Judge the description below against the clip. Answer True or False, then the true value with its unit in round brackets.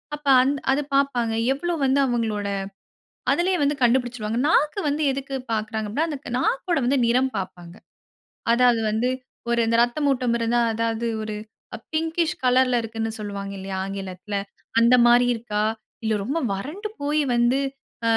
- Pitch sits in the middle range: False (245 Hz)